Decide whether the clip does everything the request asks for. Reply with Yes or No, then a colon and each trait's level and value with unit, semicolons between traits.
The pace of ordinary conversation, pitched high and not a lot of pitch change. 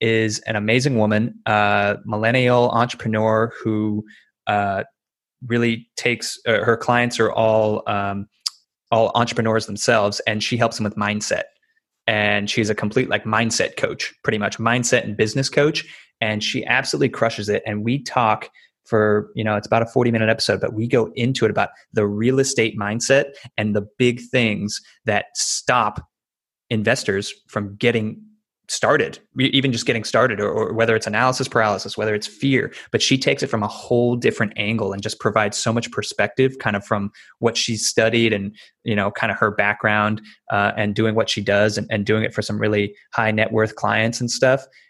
No: average, 185 wpm; low, 110 Hz; narrow, 2.1 semitones